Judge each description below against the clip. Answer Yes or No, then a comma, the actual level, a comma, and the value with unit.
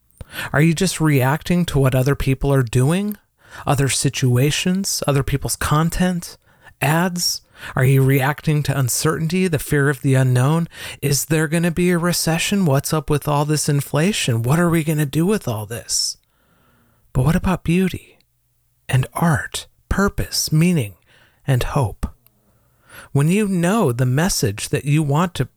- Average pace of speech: Yes, average, 155 wpm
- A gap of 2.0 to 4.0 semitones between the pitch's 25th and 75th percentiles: No, average, 4.4 semitones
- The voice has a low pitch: No, medium, 145 Hz